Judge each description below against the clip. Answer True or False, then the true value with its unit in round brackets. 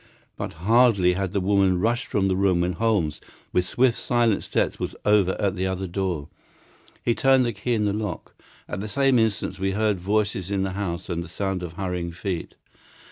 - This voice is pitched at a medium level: False (95 Hz)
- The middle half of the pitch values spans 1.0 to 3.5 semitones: True (3.1 semitones)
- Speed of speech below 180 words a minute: False (200 wpm)